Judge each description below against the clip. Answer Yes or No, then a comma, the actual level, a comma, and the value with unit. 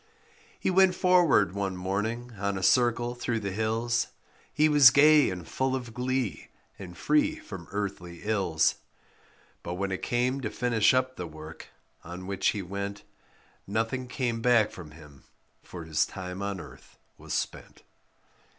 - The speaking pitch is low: Yes, low, 110 Hz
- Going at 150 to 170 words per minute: Yes, average, 155 wpm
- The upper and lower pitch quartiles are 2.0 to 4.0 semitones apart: No, average, 5.2 semitones